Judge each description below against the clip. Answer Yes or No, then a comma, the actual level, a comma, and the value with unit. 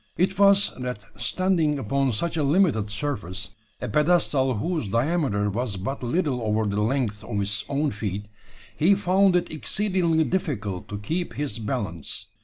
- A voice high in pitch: No, low, 135 Hz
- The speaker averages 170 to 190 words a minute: No, average, 155 wpm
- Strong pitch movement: Yes, wide, 8.4 semitones